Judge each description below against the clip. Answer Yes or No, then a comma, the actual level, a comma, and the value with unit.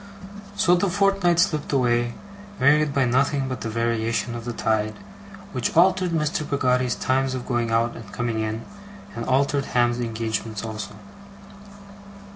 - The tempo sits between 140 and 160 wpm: Yes, average, 145 wpm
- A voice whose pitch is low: Yes, low, 125 Hz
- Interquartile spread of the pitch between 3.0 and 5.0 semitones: Yes, average, 3.9 semitones